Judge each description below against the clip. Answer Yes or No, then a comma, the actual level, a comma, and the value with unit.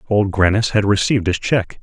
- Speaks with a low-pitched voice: Yes, low, 100 Hz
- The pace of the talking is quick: No, average, 195 wpm